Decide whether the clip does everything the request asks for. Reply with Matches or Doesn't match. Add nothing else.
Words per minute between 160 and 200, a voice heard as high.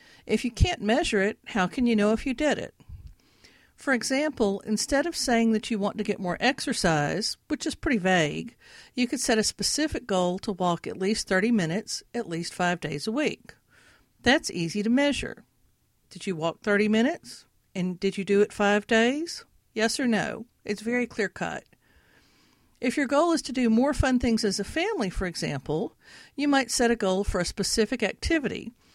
Matches